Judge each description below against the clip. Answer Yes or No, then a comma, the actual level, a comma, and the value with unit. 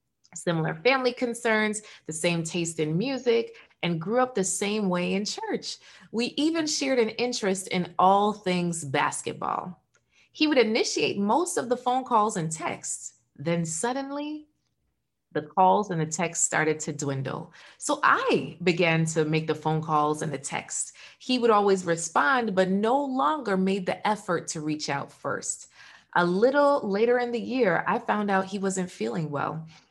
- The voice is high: Yes, high, 195 Hz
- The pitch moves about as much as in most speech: No, wide, 6.5 semitones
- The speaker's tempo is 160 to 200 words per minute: Yes, average, 165 wpm